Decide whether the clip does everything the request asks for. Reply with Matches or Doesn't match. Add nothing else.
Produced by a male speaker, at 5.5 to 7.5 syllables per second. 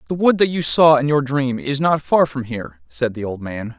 Doesn't match